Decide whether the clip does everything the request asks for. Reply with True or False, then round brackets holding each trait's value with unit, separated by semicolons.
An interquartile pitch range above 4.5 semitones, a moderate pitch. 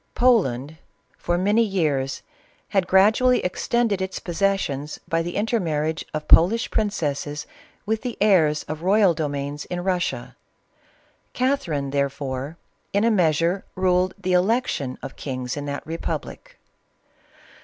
True (5.6 semitones; 175 Hz)